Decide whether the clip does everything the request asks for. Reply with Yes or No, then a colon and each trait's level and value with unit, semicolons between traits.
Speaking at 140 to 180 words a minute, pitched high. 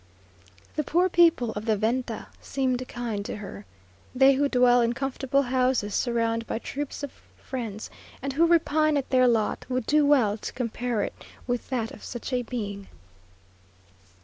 Yes: average, 165 wpm; very high, 250 Hz